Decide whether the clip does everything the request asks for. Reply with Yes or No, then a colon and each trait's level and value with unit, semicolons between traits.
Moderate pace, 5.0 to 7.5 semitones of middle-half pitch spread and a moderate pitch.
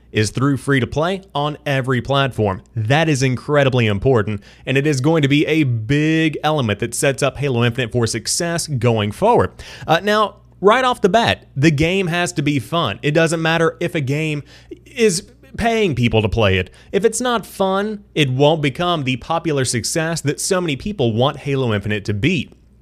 Yes: average, 190 wpm; wide, 5.4 semitones; medium, 145 Hz